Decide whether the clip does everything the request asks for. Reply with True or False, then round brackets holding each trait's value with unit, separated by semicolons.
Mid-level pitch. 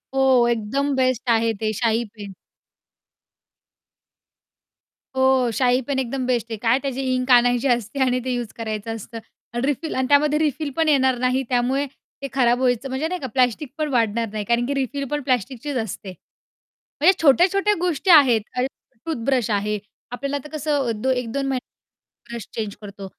False (255 Hz)